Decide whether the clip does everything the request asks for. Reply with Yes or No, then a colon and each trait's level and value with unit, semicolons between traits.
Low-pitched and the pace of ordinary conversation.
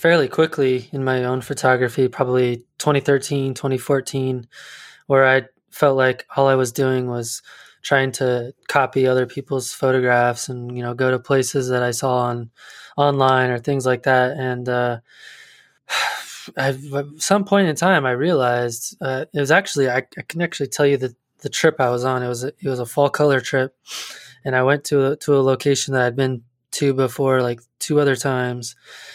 Yes: low, 130 Hz; average, 190 wpm